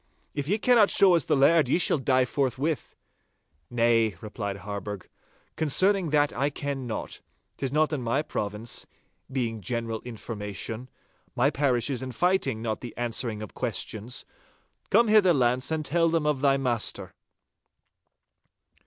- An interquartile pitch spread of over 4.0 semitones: Yes, average, 4.9 semitones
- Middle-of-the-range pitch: No, low, 130 Hz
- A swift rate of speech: No, average, 145 wpm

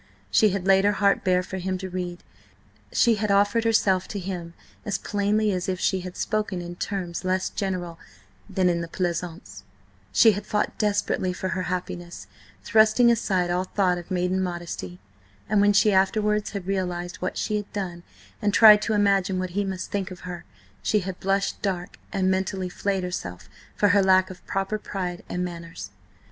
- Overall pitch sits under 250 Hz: Yes, high, 190 Hz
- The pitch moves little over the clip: Yes, narrow, 2.2 semitones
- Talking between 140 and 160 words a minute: No, average, 185 wpm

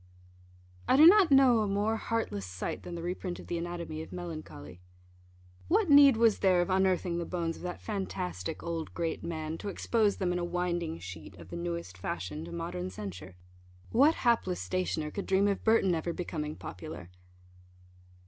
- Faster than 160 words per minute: Yes, average, 175 wpm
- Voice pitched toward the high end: No, medium, 175 Hz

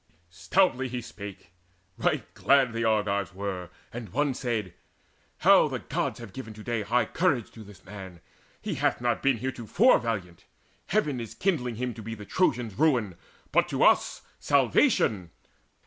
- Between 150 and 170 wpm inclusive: Yes, average, 160 wpm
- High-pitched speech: No, low, 115 Hz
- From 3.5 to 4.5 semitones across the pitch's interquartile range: Yes, average, 3.9 semitones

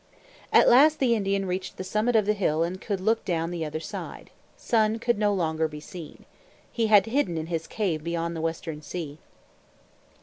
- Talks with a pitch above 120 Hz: Yes, medium, 185 Hz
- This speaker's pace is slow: No, average, 195 wpm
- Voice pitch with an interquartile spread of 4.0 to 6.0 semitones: Yes, average, 4.8 semitones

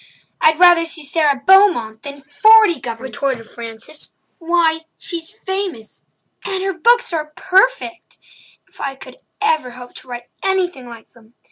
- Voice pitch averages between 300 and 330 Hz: Yes, very high, 320 Hz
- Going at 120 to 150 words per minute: Yes, average, 140 wpm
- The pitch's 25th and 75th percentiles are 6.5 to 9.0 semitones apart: Yes, wide, 7.0 semitones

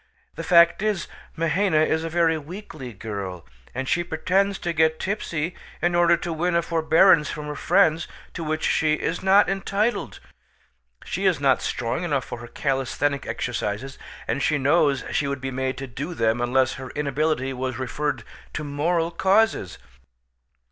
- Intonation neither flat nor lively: Yes, average, 4.5 semitones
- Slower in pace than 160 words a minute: No, average, 165 wpm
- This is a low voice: No, medium, 155 Hz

